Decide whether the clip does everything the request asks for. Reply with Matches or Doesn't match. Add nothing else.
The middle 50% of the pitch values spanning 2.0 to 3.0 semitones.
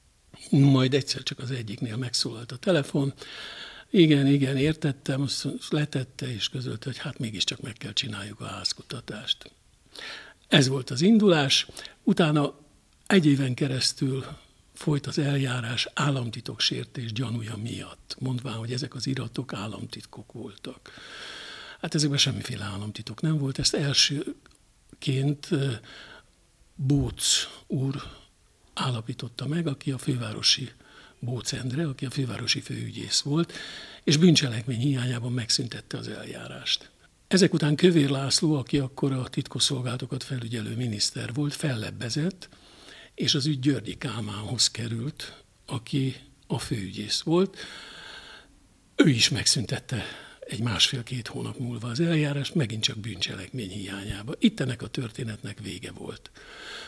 Doesn't match